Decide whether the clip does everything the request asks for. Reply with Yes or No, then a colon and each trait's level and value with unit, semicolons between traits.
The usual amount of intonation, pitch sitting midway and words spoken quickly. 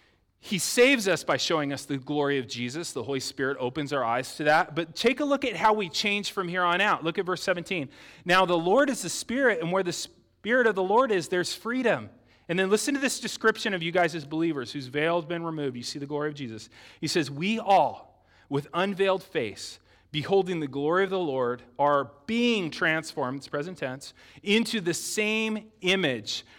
No: wide, 6.0 semitones; medium, 170 Hz; fast, 215 wpm